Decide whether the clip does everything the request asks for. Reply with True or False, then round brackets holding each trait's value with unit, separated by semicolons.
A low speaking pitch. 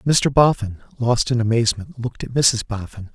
True (120 Hz)